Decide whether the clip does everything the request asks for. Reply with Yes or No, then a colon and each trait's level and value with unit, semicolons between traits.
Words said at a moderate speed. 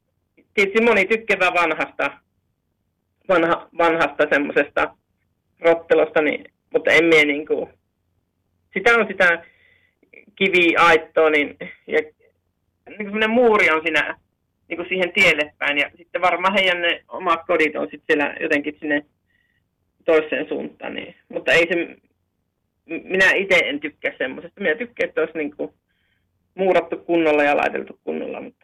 Yes: average, 130 wpm